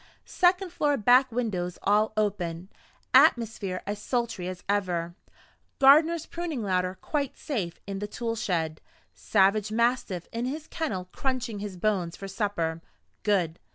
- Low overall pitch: No, high, 210 Hz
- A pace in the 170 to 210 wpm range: No, slow, 135 wpm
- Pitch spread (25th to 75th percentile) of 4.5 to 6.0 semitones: Yes, average, 5.3 semitones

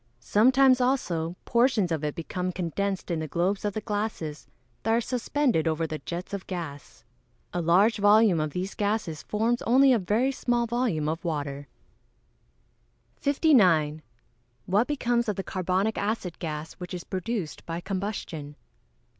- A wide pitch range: Yes, wide, 5.7 semitones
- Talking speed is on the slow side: No, average, 150 wpm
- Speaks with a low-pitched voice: No, high, 195 Hz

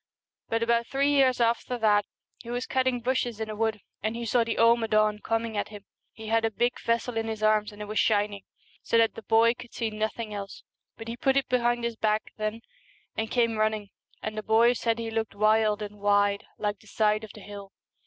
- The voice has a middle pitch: No, high, 225 Hz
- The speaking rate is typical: No, fast, 225 wpm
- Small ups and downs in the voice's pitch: Yes, narrow, 1.7 semitones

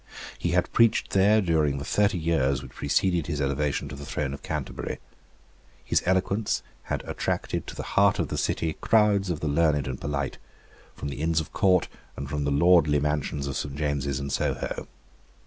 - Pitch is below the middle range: Yes, very low, 75 Hz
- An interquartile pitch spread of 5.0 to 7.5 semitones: No, average, 3.9 semitones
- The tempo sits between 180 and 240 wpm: Yes, average, 185 wpm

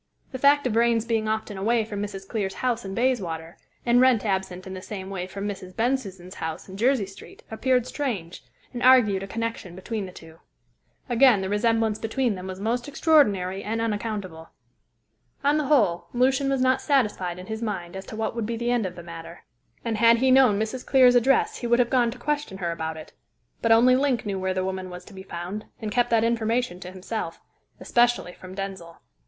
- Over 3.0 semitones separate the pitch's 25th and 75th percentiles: Yes, average, 4.4 semitones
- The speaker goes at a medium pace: No, fast, 210 wpm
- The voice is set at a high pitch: Yes, high, 220 Hz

